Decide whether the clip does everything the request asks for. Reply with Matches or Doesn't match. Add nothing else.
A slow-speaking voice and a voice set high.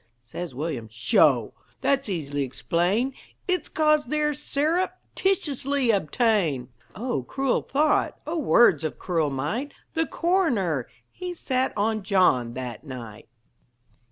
Matches